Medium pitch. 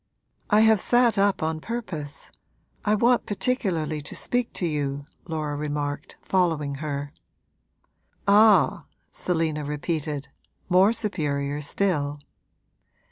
Yes: medium, 160 Hz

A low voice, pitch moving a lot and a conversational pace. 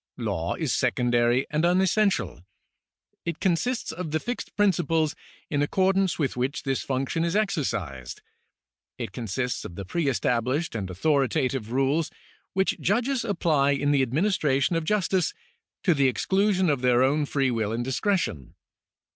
No: medium, 145 Hz; wide, 6.3 semitones; average, 145 wpm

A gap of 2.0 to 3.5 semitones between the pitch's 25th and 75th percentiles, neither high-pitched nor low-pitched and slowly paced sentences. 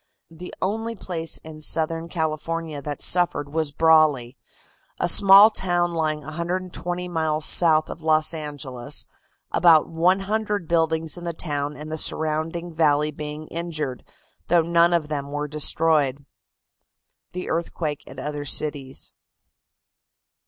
Yes: narrow, 2.4 semitones; medium, 160 Hz; slow, 125 wpm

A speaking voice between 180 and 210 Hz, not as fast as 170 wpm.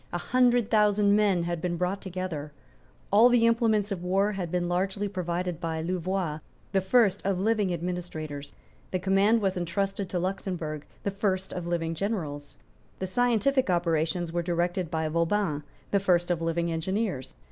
Yes: medium, 185 Hz; average, 160 wpm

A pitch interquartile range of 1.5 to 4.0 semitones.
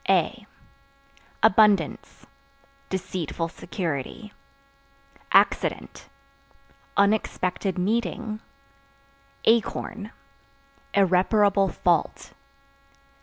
Yes: average, 3.0 semitones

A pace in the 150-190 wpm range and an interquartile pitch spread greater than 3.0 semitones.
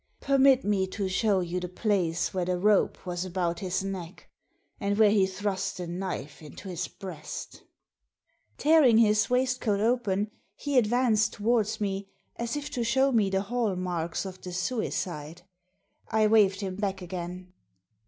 Yes: average, 155 wpm; average, 3.4 semitones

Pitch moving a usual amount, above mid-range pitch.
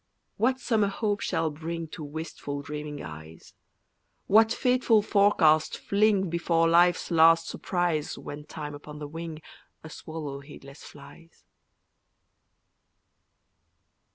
No: average, 4.7 semitones; medium, 165 Hz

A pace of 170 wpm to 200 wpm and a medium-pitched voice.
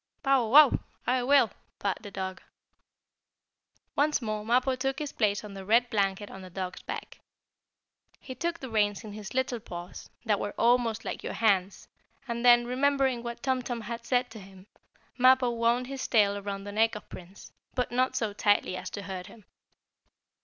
No: average, 180 wpm; high, 230 Hz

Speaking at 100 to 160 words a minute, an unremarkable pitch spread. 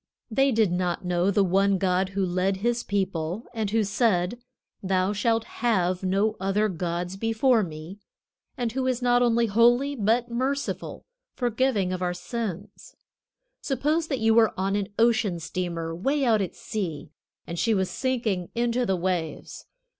Yes: average, 155 wpm; average, 4.4 semitones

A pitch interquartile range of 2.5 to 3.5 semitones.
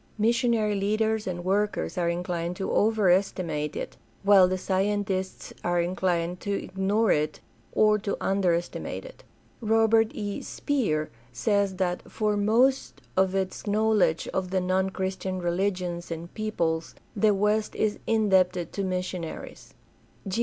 Yes: average, 2.9 semitones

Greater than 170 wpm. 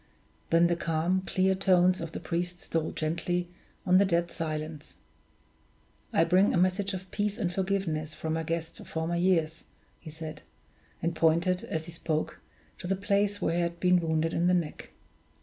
Yes: average, 180 wpm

